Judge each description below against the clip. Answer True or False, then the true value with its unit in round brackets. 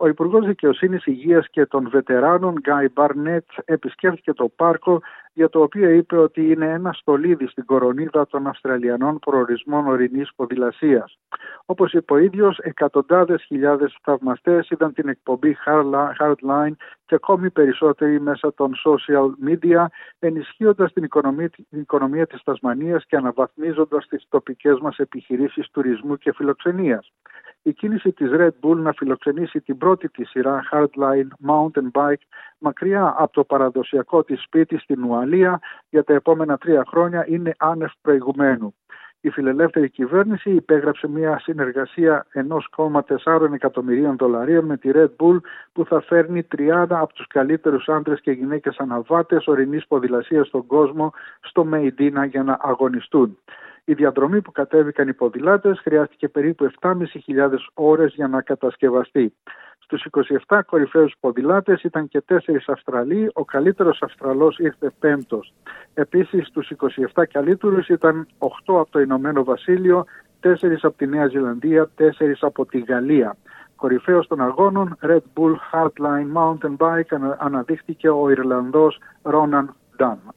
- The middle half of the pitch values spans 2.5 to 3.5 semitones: True (3.2 semitones)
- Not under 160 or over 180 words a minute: False (135 wpm)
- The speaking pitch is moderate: True (150 Hz)